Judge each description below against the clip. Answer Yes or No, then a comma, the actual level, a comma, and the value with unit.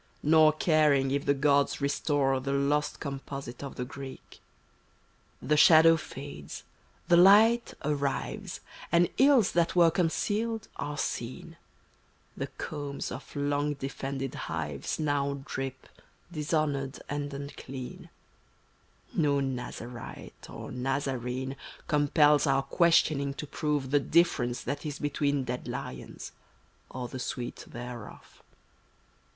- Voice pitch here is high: No, medium, 140 Hz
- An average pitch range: No, narrow, 2.3 semitones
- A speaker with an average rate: No, slow, 120 wpm